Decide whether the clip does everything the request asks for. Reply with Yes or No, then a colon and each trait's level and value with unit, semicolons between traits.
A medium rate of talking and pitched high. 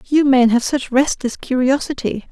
Yes: average, 155 wpm; very high, 260 Hz